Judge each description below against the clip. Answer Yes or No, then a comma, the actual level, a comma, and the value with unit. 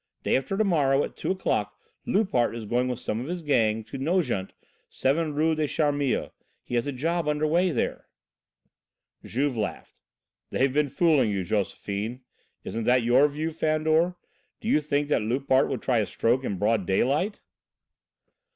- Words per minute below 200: Yes, average, 170 wpm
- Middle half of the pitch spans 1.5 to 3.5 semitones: No, average, 4.7 semitones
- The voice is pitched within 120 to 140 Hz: Yes, low, 135 Hz